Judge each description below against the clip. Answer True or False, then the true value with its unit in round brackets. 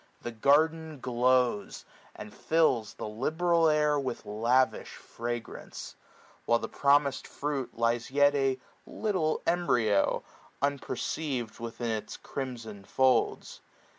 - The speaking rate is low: True (105 wpm)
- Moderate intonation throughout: True (4.1 semitones)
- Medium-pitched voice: False (130 Hz)